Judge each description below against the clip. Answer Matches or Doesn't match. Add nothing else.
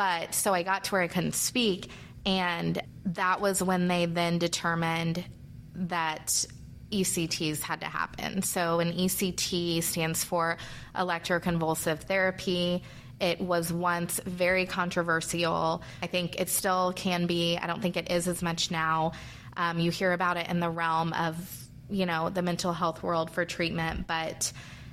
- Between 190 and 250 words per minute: Doesn't match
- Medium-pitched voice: Matches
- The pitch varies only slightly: Matches